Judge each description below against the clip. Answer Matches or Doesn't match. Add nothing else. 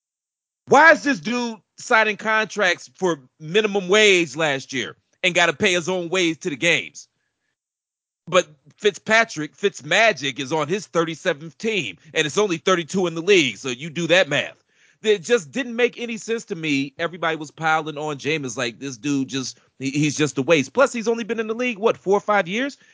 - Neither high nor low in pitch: Matches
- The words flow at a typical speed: Matches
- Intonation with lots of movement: Matches